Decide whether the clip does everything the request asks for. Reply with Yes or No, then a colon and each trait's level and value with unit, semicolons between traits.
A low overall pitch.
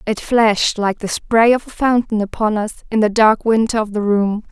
No: high, 215 Hz